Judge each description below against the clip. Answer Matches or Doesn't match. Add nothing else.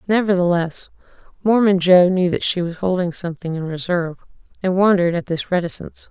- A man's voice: Doesn't match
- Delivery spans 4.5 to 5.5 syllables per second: Doesn't match